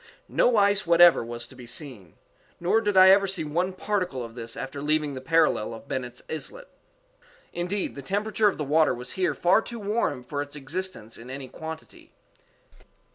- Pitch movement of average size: No, wide, 6.9 semitones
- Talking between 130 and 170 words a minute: No, average, 180 wpm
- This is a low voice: No, medium, 160 Hz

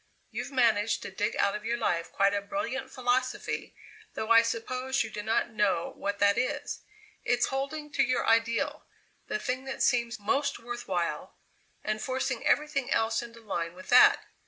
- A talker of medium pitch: No, high, 230 Hz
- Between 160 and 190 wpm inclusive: Yes, average, 175 wpm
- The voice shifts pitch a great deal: No, average, 3.6 semitones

